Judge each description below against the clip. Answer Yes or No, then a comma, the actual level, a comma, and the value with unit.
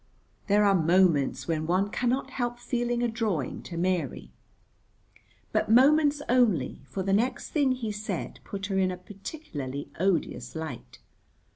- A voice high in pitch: Yes, high, 200 Hz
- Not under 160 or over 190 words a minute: No, average, 145 wpm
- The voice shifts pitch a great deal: Yes, wide, 6.2 semitones